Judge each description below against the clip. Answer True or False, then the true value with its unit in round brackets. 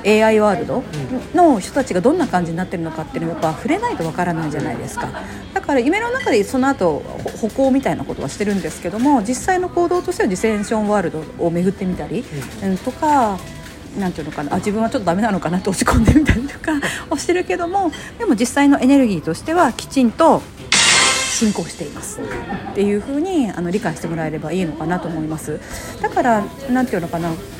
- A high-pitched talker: True (215 Hz)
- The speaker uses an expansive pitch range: True (8.6 semitones)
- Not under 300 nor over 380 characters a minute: False (450 characters per minute)